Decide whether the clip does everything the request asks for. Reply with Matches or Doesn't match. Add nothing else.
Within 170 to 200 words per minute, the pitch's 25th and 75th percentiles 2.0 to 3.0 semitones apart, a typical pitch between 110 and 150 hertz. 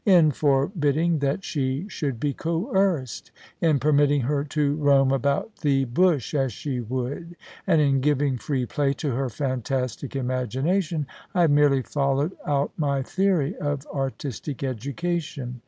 Doesn't match